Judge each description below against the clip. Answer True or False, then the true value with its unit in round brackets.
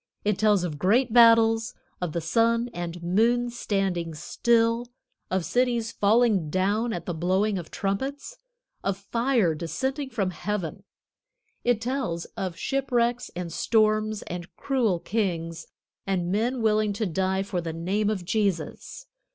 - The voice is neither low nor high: False (210 Hz)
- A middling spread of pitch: True (4.7 semitones)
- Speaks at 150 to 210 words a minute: False (140 wpm)